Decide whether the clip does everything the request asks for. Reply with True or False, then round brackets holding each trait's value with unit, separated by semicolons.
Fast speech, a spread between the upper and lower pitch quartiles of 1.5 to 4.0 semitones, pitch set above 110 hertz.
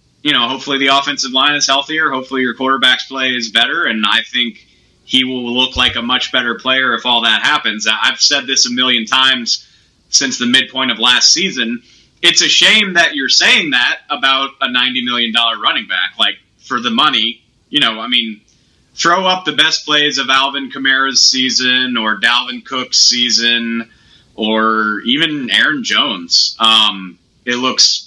False (175 wpm; 2.7 semitones; 125 Hz)